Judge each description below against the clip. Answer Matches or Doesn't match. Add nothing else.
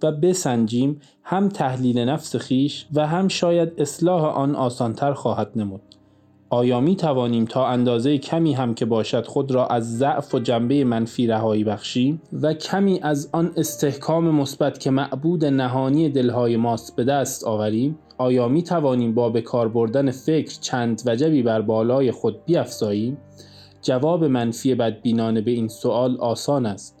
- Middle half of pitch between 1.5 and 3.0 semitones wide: Doesn't match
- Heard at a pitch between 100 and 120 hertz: Doesn't match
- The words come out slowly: Doesn't match